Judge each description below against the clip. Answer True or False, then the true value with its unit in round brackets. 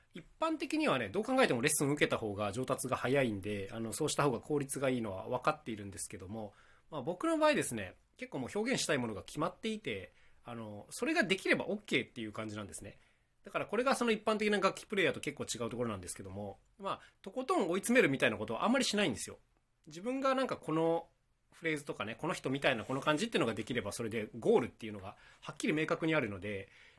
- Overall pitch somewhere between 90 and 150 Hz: True (140 Hz)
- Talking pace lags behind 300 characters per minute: False (505 characters per minute)